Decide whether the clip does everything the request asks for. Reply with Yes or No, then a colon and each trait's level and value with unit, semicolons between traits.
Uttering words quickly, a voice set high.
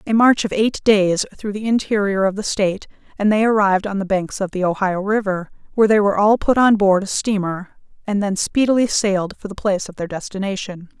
Yes: fast, 220 wpm; high, 200 Hz